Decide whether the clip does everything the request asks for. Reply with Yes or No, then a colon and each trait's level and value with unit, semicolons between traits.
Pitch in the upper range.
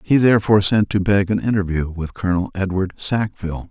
No: very low, 95 Hz